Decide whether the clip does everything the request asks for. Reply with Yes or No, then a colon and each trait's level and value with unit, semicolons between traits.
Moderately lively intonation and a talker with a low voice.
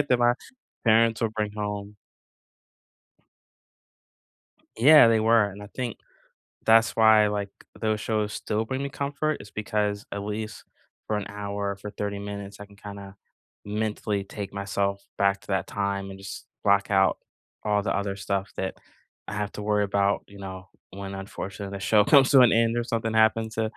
No: narrow, 1.8 semitones; low, 105 Hz